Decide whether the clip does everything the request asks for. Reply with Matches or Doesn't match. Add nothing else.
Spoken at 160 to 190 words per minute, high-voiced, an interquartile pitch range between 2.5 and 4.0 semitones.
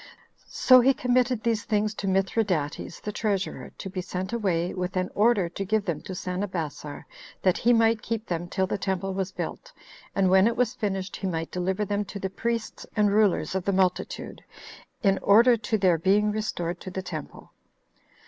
Matches